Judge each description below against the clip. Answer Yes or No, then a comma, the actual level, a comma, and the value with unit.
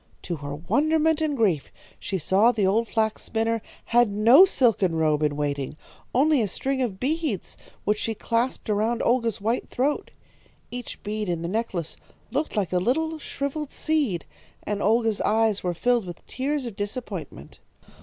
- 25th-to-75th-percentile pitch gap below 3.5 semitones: No, average, 5.3 semitones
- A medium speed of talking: Yes, average, 165 wpm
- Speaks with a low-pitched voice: No, high, 225 Hz